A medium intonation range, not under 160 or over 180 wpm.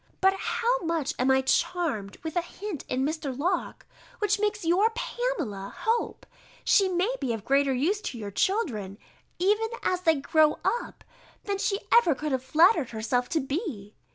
No: wide, 7.3 semitones; average, 170 wpm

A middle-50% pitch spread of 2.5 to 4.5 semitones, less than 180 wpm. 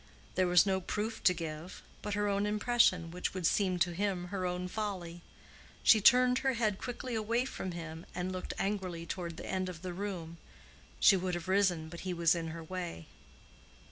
No: average, 3.1 semitones; average, 195 wpm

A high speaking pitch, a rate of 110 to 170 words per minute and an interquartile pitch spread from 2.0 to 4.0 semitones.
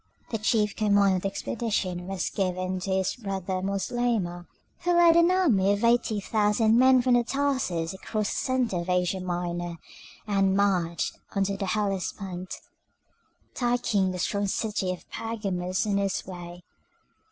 Yes: high, 195 Hz; average, 145 wpm; average, 3.5 semitones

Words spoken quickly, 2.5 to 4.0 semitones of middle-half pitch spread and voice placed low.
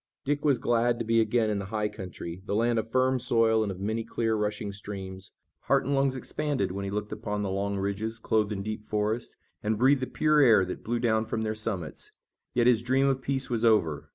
Yes: fast, 230 wpm; average, 2.9 semitones; low, 110 Hz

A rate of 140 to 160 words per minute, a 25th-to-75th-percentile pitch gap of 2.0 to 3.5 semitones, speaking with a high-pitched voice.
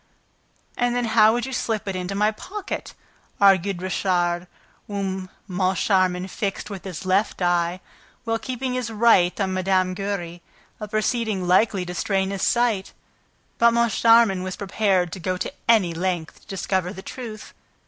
Yes: average, 155 wpm; average, 3.1 semitones; high, 195 Hz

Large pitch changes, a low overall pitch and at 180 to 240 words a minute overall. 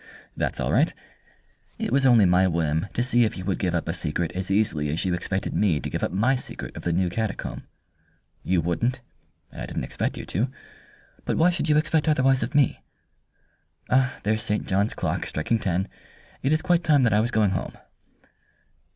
Yes: wide, 6.5 semitones; low, 105 Hz; average, 200 wpm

